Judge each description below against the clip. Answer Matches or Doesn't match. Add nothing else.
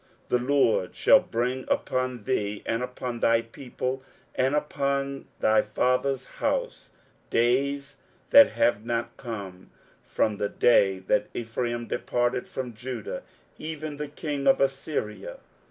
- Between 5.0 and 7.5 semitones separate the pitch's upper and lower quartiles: Doesn't match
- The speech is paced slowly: Matches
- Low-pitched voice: Matches